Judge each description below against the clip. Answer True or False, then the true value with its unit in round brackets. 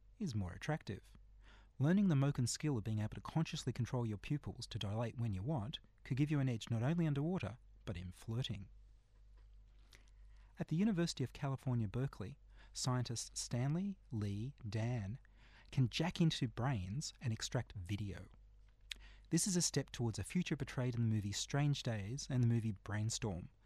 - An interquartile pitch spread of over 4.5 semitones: True (4.9 semitones)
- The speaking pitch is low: True (115 Hz)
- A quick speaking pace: False (165 wpm)